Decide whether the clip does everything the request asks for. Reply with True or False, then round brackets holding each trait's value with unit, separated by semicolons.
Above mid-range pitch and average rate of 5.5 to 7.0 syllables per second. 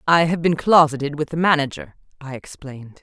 False (145 Hz; 5.6 syllables/s)